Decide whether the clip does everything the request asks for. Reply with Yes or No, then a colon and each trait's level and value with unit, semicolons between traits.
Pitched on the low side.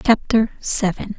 No: high, 205 Hz